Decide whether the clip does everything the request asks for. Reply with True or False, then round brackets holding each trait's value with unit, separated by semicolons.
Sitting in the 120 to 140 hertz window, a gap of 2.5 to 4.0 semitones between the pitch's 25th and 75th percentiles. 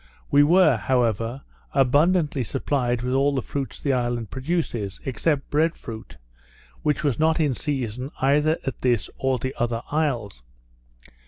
True (135 Hz; 3.6 semitones)